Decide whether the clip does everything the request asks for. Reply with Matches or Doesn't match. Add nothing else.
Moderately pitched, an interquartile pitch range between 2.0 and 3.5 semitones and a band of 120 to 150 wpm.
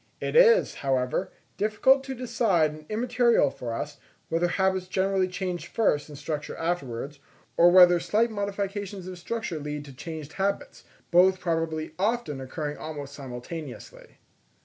Doesn't match